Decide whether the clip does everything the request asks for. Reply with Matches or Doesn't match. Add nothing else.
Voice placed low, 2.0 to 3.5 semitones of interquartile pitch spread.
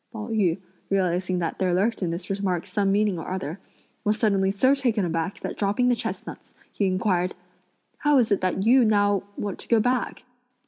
Doesn't match